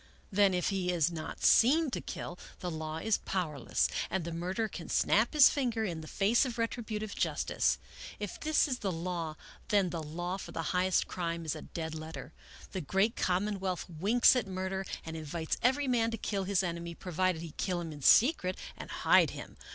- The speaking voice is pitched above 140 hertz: Yes, medium, 185 Hz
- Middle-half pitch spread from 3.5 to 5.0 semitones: Yes, average, 4.4 semitones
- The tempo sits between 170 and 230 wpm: Yes, average, 200 wpm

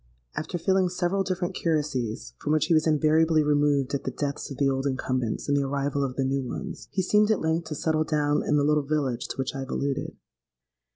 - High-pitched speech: No, medium, 150 Hz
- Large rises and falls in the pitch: No, average, 2.8 semitones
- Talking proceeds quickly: Yes, fast, 225 wpm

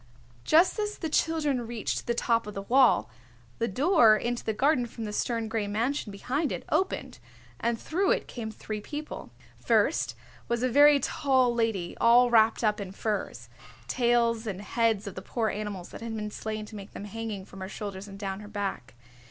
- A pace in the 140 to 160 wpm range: No, average, 195 wpm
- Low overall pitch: No, high, 225 Hz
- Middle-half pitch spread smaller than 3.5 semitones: Yes, average, 3.1 semitones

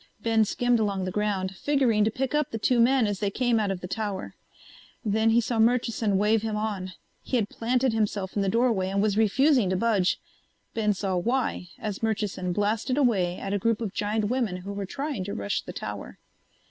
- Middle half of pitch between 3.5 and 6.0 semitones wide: No, average, 2.9 semitones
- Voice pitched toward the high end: Yes, high, 215 Hz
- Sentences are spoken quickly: Yes, fast, 210 wpm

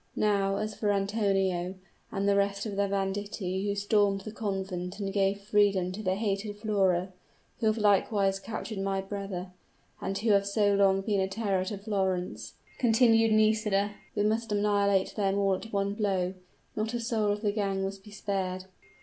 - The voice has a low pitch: No, high, 200 Hz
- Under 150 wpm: No, average, 175 wpm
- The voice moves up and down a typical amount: No, narrow, 1.5 semitones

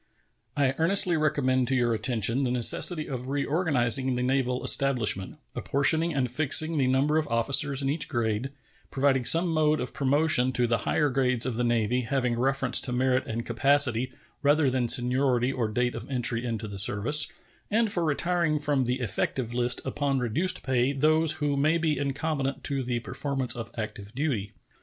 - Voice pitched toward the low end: Yes, low, 130 Hz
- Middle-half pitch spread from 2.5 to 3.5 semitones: Yes, average, 3.2 semitones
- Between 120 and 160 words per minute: No, average, 175 wpm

